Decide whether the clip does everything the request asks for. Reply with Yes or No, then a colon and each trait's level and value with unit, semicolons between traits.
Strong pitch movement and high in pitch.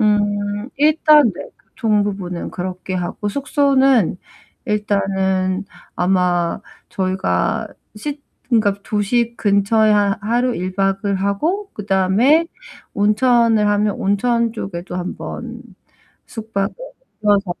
No: average, 3.5 semitones; high, 205 Hz